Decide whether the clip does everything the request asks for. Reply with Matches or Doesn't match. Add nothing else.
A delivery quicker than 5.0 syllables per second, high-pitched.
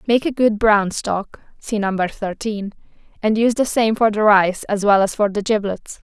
Doesn't match